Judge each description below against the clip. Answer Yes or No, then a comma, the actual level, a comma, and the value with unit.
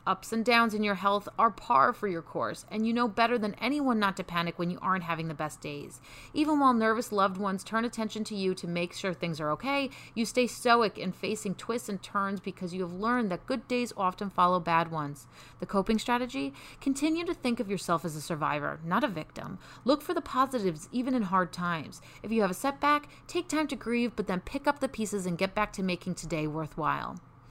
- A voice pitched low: No, high, 205 Hz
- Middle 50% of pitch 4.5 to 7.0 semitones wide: Yes, average, 5.3 semitones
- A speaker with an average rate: No, fast, 230 wpm